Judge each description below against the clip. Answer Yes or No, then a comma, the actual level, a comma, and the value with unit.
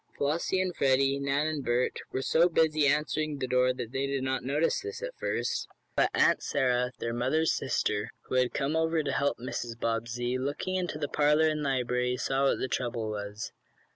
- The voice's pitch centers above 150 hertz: No, low, 135 Hz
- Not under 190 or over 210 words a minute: Yes, average, 195 wpm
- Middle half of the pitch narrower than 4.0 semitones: Yes, average, 3.6 semitones